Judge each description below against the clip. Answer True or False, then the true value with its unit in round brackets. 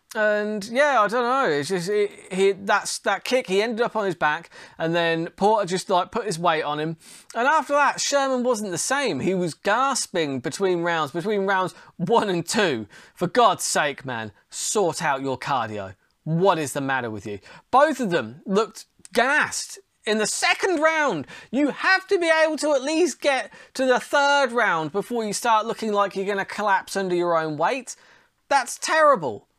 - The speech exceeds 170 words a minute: True (195 wpm)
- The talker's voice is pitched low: False (205 Hz)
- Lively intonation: True (7.2 semitones)